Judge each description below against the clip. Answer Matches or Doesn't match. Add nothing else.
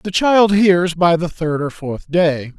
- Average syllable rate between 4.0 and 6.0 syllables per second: Doesn't match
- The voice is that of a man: Matches